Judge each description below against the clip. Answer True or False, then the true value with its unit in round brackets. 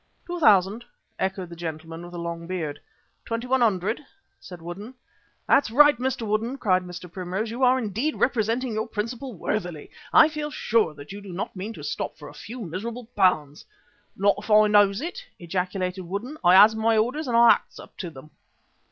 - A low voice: False (210 Hz)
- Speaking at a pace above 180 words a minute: True (190 wpm)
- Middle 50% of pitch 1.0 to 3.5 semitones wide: False (4.7 semitones)